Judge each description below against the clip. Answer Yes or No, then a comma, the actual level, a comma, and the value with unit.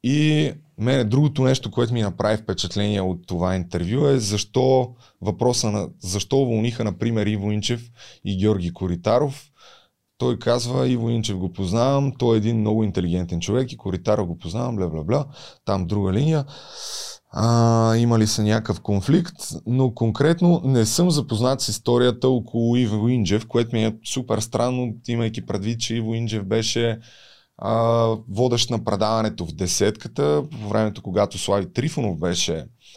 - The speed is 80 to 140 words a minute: No, average, 150 wpm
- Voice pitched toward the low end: Yes, low, 115 Hz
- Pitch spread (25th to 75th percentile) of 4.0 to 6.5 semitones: No, average, 3.3 semitones